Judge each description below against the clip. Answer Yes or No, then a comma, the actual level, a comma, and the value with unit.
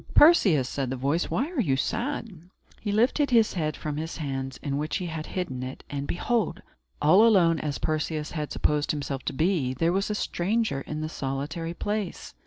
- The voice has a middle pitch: Yes, medium, 160 Hz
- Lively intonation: Yes, wide, 6.0 semitones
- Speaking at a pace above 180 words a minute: Yes, average, 195 wpm